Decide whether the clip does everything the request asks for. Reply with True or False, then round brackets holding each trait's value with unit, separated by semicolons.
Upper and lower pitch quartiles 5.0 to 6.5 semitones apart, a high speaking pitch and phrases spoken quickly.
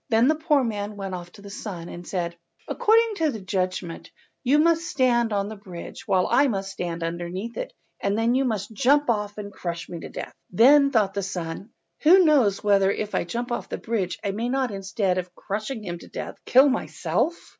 True (5.3 semitones; 210 Hz; 210 wpm)